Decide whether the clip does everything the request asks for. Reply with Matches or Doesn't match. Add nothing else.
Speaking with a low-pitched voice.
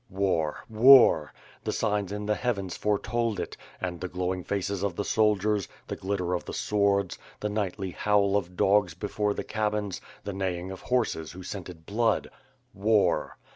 Matches